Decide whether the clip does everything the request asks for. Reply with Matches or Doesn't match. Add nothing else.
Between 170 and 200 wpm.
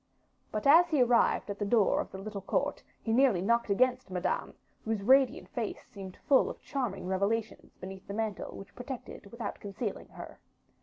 Matches